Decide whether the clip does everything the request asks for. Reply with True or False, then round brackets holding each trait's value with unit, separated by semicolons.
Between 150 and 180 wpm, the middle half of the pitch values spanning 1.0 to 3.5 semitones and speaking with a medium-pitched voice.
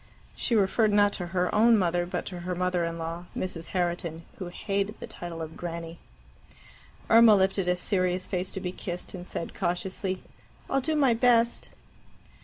True (175 wpm; 2.7 semitones; 180 Hz)